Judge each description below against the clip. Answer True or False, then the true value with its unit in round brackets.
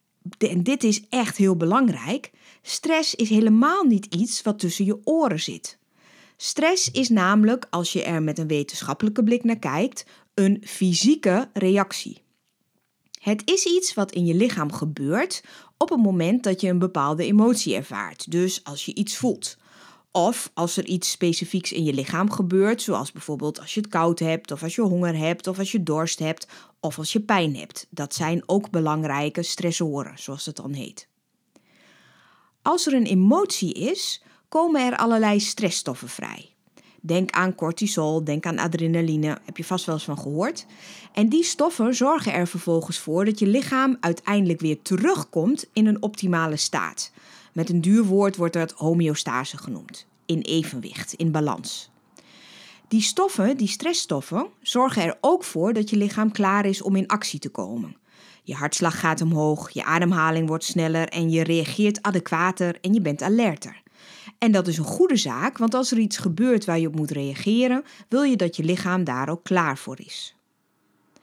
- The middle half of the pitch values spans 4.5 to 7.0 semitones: True (5.1 semitones)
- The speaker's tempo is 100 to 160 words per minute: False (175 wpm)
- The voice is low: False (185 Hz)